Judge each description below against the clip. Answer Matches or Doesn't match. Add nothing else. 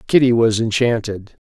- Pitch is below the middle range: Matches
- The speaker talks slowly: Matches